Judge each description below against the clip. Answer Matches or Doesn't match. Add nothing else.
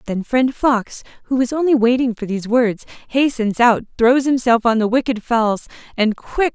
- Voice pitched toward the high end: Matches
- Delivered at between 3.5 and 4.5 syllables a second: Doesn't match